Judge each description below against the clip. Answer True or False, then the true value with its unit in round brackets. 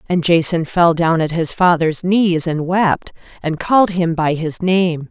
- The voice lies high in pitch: False (170 Hz)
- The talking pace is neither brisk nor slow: True (190 wpm)